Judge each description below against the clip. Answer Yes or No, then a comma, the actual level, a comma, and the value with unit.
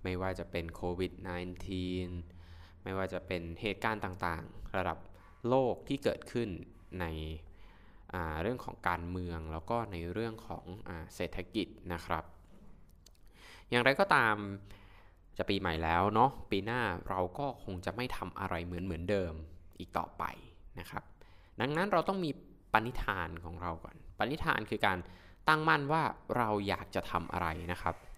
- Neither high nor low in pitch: No, very low, 90 Hz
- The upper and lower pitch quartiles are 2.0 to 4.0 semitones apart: Yes, average, 3.4 semitones